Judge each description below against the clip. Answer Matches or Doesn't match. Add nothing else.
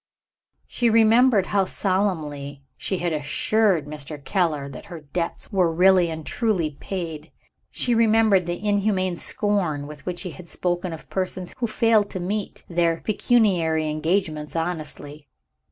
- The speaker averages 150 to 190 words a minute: Doesn't match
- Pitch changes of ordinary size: Matches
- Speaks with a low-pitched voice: Doesn't match